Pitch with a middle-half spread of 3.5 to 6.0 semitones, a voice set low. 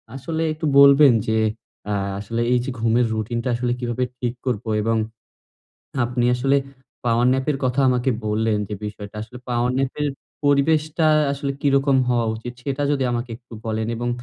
No: average, 3.0 semitones; low, 125 Hz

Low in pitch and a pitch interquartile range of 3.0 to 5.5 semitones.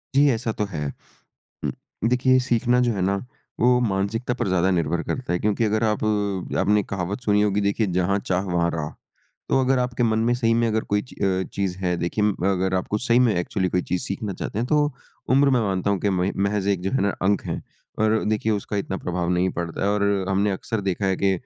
Yes: low, 100 Hz; average, 3.3 semitones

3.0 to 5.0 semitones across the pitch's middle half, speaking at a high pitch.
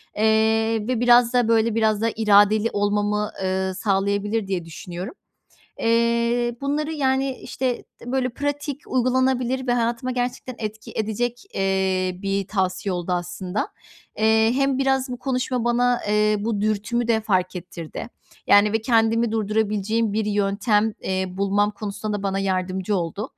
Yes: average, 3.3 semitones; high, 220 Hz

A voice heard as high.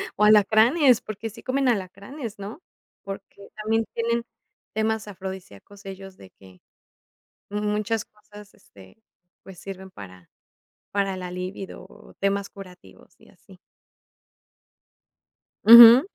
Yes: high, 200 Hz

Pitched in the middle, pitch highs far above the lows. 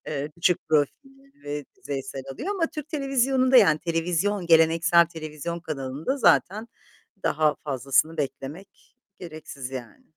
Yes: medium, 165 Hz; wide, 7.1 semitones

